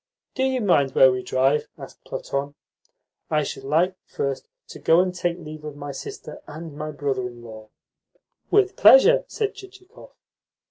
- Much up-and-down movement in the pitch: Yes, wide, 5.8 semitones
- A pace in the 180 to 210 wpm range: No, average, 165 wpm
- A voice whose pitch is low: No, medium, 150 Hz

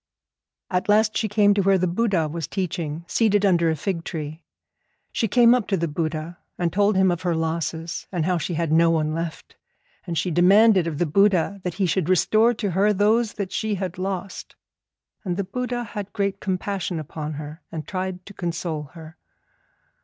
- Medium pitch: Yes, medium, 180 Hz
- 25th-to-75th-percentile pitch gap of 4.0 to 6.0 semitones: No, average, 3.5 semitones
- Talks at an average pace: Yes, average, 190 wpm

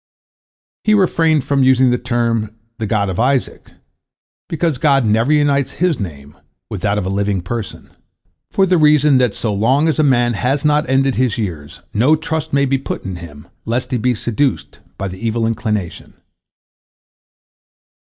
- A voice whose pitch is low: Yes, low, 125 Hz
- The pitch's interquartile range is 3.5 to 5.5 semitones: Yes, average, 5.2 semitones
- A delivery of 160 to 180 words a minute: Yes, average, 170 wpm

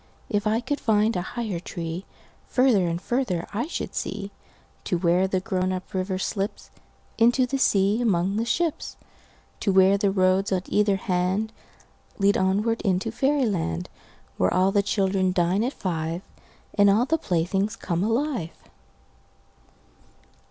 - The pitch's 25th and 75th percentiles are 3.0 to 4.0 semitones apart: Yes, average, 3.4 semitones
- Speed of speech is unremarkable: No, slow, 130 wpm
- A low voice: No, high, 195 Hz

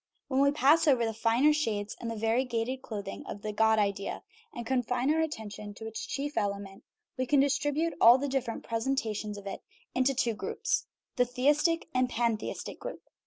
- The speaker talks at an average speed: Yes, average, 195 wpm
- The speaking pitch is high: Yes, high, 245 Hz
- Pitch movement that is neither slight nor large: Yes, average, 4.1 semitones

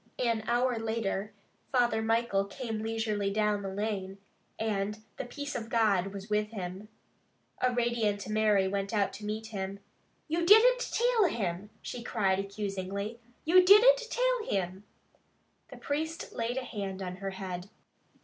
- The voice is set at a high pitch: Yes, high, 215 Hz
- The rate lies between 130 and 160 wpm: Yes, average, 150 wpm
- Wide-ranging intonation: No, average, 3.6 semitones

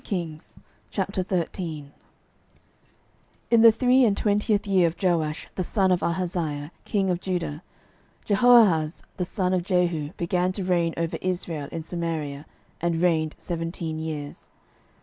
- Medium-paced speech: No, slow, 130 wpm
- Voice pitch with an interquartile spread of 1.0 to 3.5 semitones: Yes, average, 2.8 semitones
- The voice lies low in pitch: No, medium, 175 Hz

